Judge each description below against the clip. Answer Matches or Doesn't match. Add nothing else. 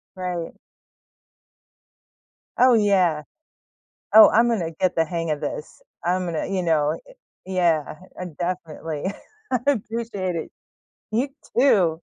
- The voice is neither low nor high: Matches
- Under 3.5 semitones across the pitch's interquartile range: Doesn't match